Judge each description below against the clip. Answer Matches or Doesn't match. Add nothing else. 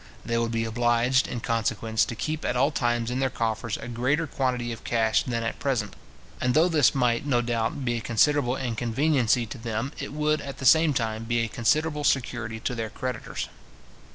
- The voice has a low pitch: Matches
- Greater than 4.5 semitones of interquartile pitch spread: Doesn't match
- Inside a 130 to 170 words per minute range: Doesn't match